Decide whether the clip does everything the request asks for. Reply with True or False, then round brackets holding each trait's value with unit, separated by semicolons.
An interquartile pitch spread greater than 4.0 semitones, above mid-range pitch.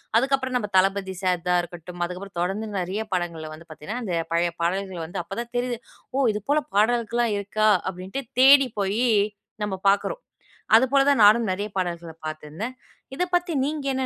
True (5.3 semitones; 200 Hz)